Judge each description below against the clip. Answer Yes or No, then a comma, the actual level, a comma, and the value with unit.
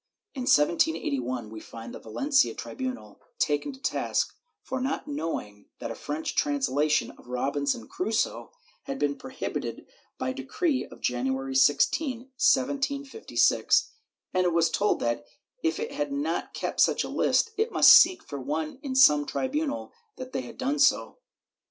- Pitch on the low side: No, medium, 165 Hz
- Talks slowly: No, average, 150 wpm